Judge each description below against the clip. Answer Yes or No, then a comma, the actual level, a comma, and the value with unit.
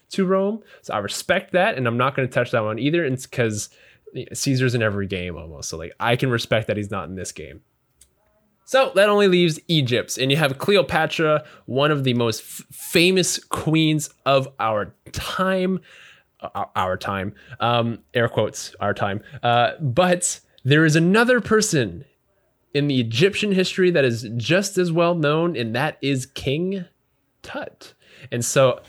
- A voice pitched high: No, medium, 140 Hz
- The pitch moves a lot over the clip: Yes, wide, 7.0 semitones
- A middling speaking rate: Yes, average, 170 wpm